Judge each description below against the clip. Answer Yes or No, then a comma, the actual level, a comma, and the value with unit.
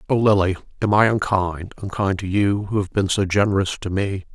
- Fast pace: No, average, 195 wpm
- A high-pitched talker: No, low, 100 Hz